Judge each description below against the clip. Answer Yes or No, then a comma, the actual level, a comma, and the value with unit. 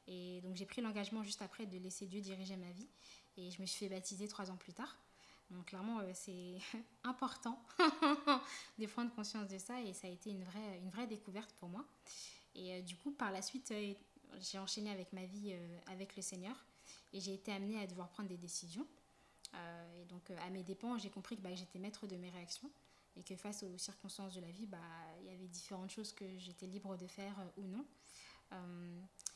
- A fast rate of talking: No, average, 200 wpm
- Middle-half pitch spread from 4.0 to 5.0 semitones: No, narrow, 2.6 semitones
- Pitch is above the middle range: Yes, high, 195 Hz